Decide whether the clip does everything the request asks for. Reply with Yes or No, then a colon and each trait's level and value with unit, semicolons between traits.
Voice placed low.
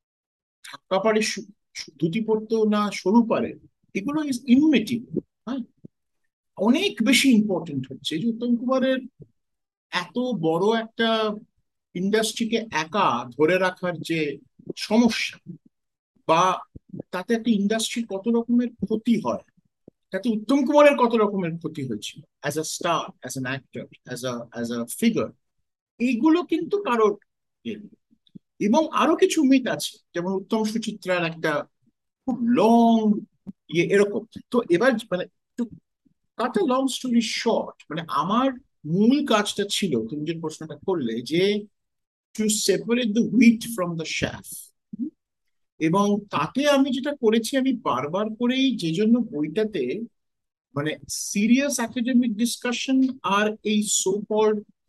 No: high, 220 Hz